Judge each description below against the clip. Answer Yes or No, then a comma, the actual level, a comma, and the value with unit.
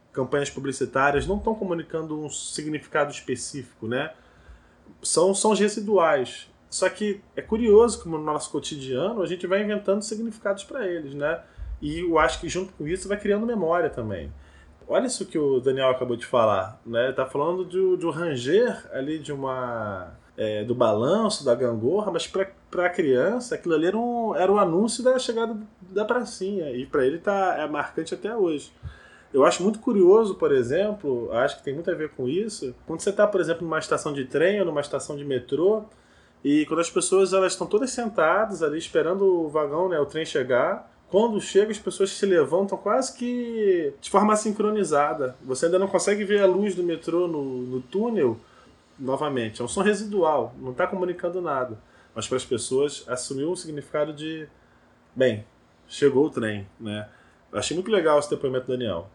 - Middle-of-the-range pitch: Yes, medium, 175 Hz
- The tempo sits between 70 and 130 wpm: No, fast, 185 wpm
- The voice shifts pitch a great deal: Yes, wide, 6.7 semitones